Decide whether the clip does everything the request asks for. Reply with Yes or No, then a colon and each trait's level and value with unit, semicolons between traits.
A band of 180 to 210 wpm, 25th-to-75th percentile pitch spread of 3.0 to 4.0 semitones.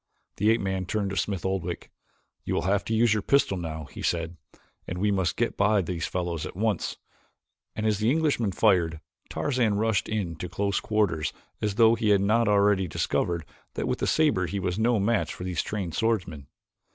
Yes: average, 200 wpm; average, 3.5 semitones